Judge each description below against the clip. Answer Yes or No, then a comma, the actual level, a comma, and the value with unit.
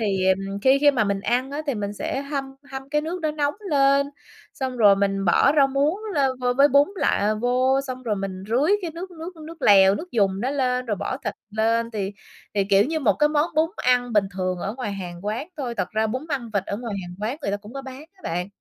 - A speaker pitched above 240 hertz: Yes, very high, 250 Hz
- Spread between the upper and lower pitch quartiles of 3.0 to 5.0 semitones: No, wide, 5.6 semitones